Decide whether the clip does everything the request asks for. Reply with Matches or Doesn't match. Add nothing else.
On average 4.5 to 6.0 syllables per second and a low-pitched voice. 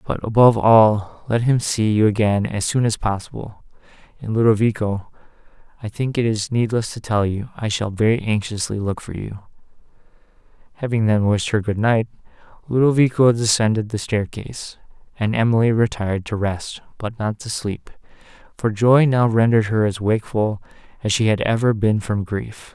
Matches